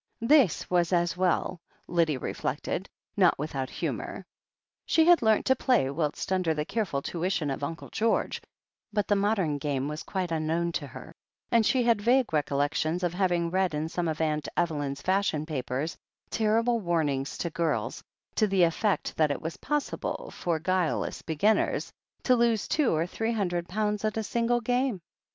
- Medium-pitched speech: Yes, medium, 175 Hz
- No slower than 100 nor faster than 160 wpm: No, average, 170 wpm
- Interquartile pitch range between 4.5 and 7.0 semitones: Yes, wide, 5.6 semitones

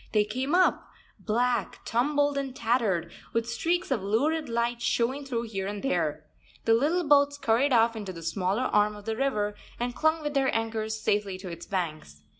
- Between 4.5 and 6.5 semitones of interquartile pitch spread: Yes, average, 4.8 semitones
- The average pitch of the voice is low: No, high, 230 Hz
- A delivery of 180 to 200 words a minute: Yes, average, 185 wpm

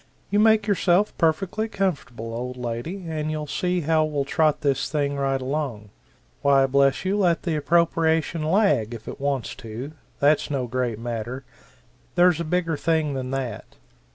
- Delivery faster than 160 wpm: No, average, 155 wpm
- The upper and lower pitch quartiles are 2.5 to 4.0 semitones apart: No, average, 4.7 semitones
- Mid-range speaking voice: Yes, medium, 150 Hz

